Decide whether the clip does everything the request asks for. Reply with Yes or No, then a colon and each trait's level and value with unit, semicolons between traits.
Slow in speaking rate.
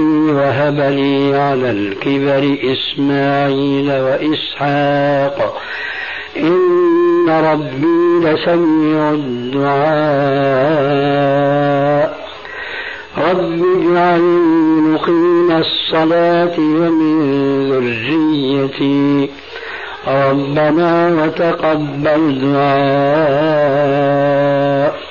Yes: slow, 45 wpm